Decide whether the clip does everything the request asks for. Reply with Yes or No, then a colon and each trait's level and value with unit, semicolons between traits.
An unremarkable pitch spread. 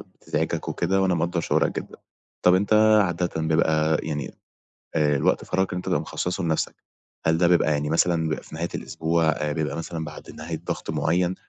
No: narrow, 2.1 semitones